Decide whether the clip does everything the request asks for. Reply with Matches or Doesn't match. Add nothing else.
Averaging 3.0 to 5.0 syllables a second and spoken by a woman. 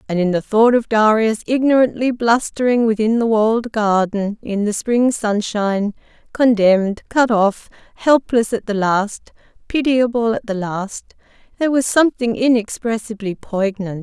Matches